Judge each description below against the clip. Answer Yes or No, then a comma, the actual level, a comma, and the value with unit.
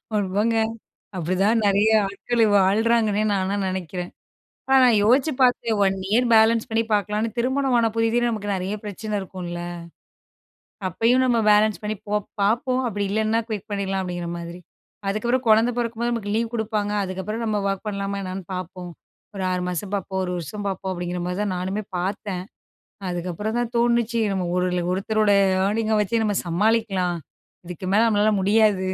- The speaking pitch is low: No, high, 205 Hz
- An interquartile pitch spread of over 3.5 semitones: No, average, 3.2 semitones